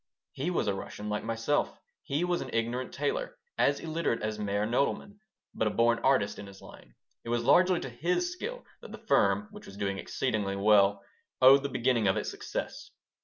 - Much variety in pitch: Yes, wide, 6.7 semitones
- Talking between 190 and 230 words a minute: Yes, average, 195 wpm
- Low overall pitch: Yes, low, 120 Hz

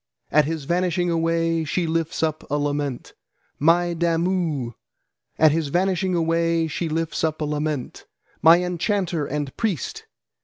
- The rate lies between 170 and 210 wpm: No, average, 140 wpm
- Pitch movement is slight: Yes, narrow, 2.3 semitones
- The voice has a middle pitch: Yes, medium, 165 Hz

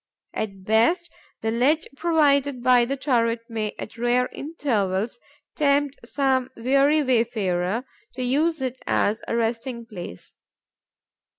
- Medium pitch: No, high, 245 Hz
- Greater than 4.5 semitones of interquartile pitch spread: No, average, 3.7 semitones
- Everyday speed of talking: No, slow, 120 wpm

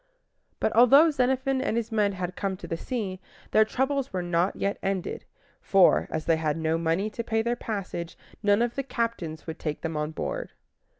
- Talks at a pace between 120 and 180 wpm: No, average, 195 wpm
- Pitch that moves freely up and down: Yes, wide, 5.8 semitones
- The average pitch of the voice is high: Yes, high, 200 Hz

